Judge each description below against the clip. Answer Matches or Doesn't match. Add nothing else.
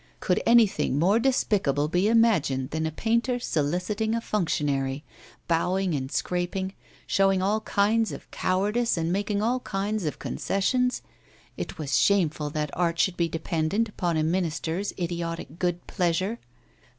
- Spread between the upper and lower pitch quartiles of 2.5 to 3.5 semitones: Doesn't match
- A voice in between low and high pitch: Matches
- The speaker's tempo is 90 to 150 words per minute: Matches